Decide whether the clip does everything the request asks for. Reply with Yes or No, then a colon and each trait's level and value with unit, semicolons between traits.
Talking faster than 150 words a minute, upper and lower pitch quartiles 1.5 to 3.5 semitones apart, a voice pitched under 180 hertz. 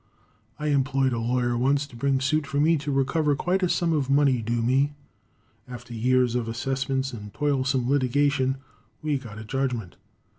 Yes: average, 175 wpm; average, 2.7 semitones; low, 135 Hz